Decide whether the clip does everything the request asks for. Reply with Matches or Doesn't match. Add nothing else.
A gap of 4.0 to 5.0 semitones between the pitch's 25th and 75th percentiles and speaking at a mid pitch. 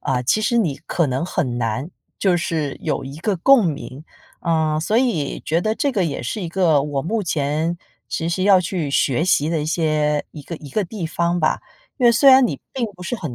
Matches